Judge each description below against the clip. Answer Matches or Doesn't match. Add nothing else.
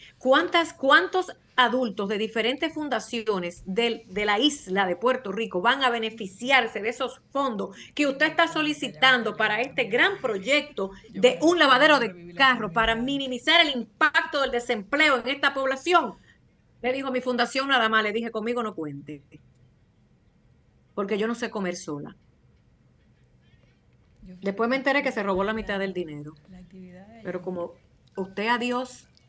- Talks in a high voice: Matches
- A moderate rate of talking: Matches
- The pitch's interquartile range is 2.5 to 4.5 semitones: Doesn't match